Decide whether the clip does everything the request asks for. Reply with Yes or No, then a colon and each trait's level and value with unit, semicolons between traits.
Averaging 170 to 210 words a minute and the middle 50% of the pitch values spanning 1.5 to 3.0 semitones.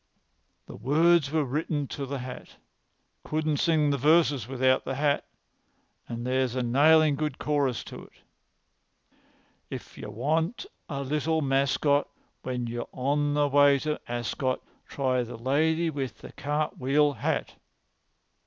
No: average, 140 wpm; average, 2.7 semitones